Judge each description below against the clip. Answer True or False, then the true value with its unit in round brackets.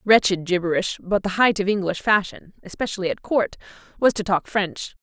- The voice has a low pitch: False (195 Hz)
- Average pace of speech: True (180 wpm)